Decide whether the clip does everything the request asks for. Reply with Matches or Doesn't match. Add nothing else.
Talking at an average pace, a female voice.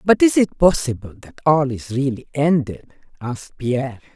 Matches